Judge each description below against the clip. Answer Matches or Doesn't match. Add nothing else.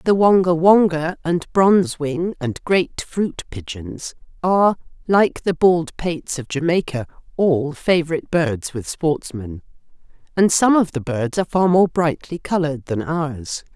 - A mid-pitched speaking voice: Matches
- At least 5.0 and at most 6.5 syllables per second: Doesn't match